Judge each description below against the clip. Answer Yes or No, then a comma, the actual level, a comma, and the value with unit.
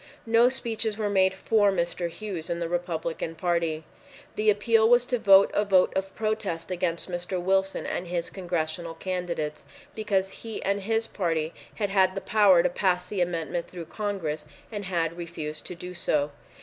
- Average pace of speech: Yes, average, 175 wpm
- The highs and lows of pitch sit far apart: No, average, 3.2 semitones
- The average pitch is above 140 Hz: Yes, medium, 185 Hz